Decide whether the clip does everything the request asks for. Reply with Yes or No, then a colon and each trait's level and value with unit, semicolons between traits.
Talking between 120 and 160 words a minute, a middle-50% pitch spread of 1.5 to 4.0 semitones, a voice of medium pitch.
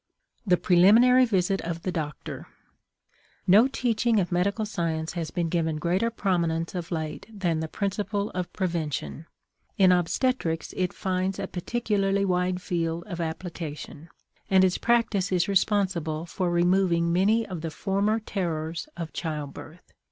Yes: average, 140 wpm; average, 3.2 semitones; medium, 180 Hz